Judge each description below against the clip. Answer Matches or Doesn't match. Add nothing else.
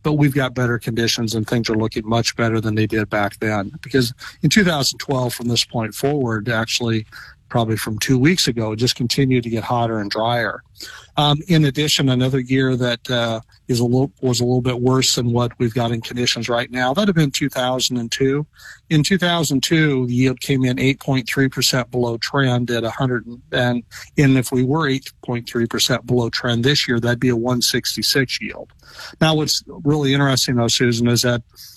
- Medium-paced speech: Matches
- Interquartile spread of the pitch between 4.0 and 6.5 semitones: Doesn't match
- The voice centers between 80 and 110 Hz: Doesn't match